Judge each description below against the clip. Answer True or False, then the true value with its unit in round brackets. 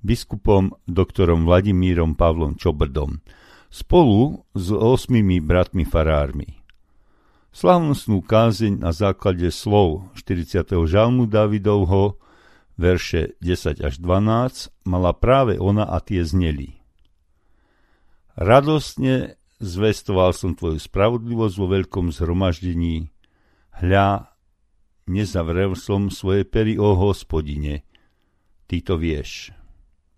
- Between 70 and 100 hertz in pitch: True (95 Hz)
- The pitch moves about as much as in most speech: True (3.7 semitones)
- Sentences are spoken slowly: True (90 wpm)